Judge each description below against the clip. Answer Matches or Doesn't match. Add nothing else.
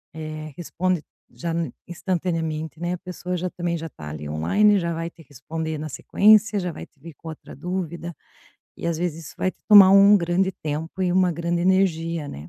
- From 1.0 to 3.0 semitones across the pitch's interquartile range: Matches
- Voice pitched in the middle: Matches